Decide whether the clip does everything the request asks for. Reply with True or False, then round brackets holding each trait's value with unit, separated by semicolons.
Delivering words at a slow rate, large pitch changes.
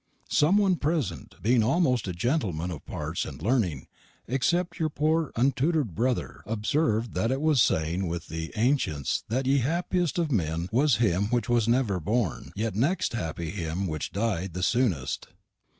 False (165 wpm; 7.6 semitones)